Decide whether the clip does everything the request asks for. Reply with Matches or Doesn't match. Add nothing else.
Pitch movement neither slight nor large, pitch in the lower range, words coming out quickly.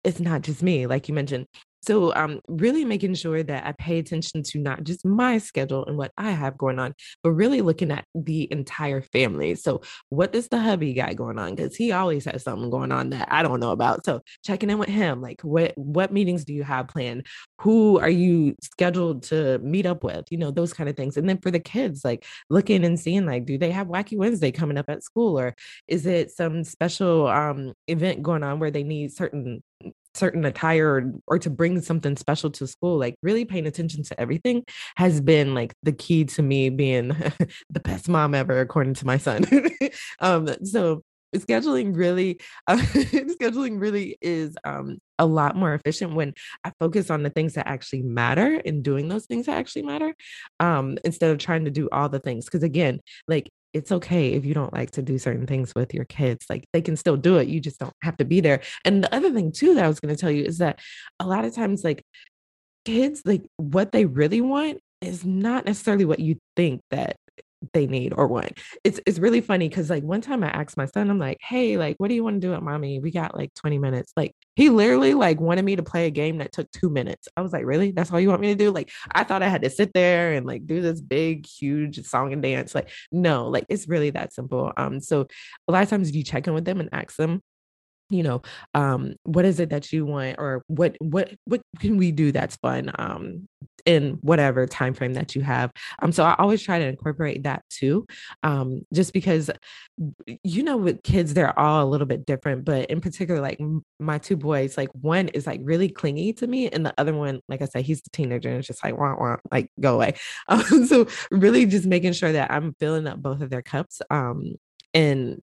Doesn't match